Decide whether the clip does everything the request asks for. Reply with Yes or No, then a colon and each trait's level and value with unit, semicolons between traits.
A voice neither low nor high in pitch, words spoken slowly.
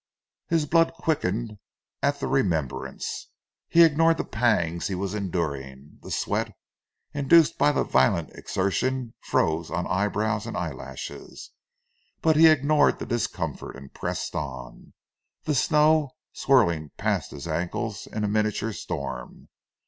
No: low, 105 Hz; slow, 130 wpm